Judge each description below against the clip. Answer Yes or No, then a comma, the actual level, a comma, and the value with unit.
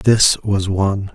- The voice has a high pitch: No, low, 100 Hz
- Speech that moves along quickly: No, average, 155 wpm